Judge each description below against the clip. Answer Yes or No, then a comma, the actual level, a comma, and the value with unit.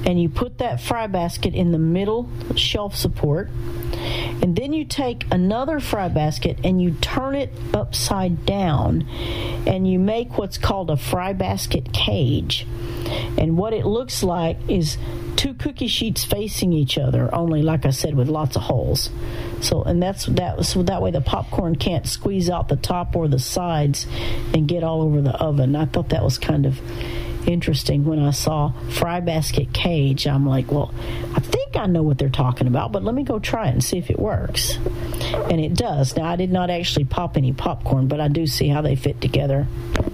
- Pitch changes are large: Yes, wide, 6.2 semitones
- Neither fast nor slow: Yes, average, 195 wpm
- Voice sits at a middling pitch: Yes, medium, 145 Hz